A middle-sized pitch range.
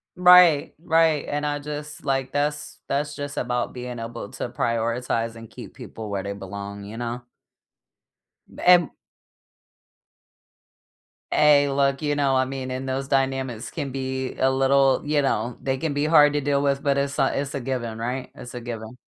Yes: average, 3.0 semitones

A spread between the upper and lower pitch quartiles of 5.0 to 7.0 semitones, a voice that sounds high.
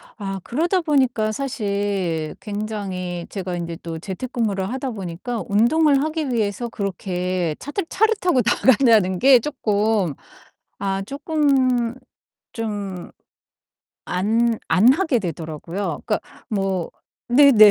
Yes: wide, 5.5 semitones; high, 215 Hz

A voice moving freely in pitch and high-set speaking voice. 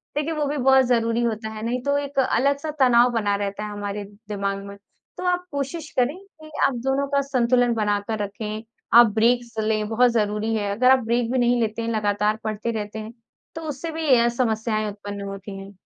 No: average, 3.9 semitones; high, 230 Hz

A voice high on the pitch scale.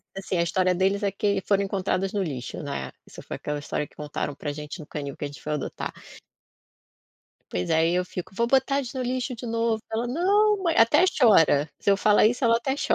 Yes: high, 195 Hz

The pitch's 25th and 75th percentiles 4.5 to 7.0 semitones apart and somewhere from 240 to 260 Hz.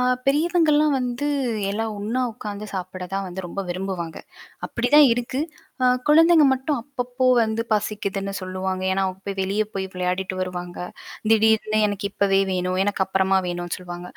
No: average, 4.8 semitones; high, 200 Hz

